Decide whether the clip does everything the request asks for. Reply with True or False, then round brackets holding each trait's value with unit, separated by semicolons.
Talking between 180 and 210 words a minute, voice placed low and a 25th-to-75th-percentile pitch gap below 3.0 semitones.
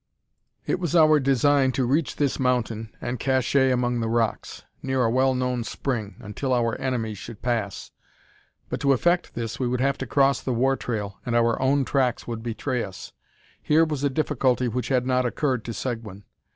True (190 wpm; 125 Hz; 2.6 semitones)